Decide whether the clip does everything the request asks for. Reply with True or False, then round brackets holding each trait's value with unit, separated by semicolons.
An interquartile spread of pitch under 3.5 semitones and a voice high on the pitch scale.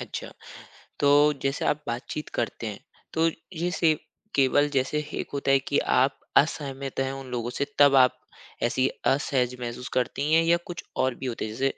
False (2.4 semitones; 135 Hz)